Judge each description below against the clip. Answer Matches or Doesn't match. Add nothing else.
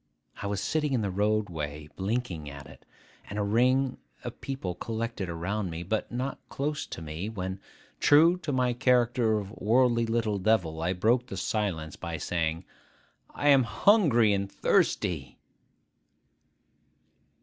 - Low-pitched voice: Matches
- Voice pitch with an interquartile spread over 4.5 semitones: Matches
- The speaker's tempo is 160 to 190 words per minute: Doesn't match